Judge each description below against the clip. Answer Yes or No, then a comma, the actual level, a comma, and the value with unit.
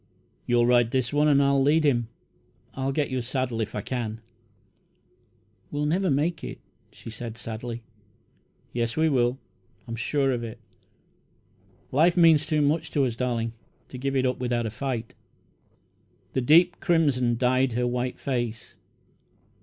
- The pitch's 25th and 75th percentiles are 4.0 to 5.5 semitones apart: No, average, 3.5 semitones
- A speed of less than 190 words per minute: Yes, average, 155 wpm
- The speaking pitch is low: Yes, low, 130 Hz